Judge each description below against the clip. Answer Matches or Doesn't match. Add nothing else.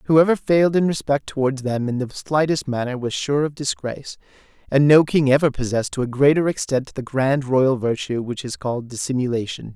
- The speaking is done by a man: Matches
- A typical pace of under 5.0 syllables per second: Doesn't match